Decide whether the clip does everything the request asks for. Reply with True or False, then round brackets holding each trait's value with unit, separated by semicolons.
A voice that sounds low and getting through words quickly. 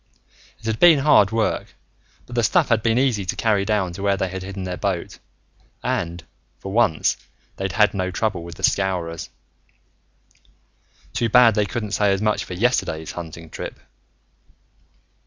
False (100 Hz; 165 wpm)